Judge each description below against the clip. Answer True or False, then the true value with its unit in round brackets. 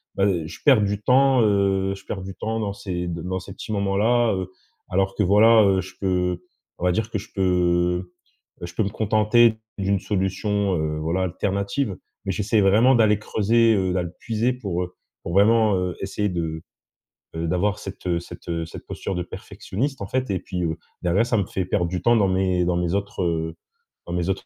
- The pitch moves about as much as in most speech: True (3.0 semitones)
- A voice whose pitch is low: True (95 Hz)